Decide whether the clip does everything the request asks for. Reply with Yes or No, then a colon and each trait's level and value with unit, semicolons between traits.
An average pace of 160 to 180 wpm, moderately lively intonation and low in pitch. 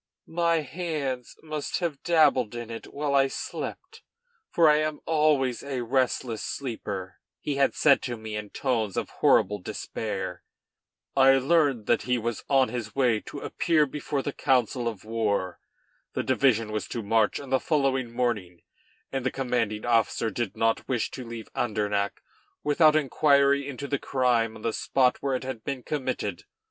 Yes: average, 165 wpm; average, 3.8 semitones; low, 130 Hz